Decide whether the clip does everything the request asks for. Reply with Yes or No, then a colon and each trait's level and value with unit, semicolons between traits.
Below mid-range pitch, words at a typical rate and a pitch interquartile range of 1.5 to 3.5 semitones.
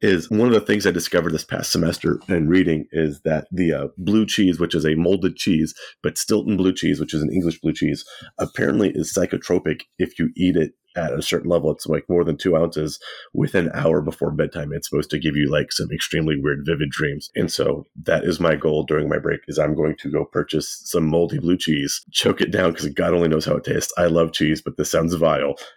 No: very low, 85 Hz; fast, 240 wpm; narrow, 2.6 semitones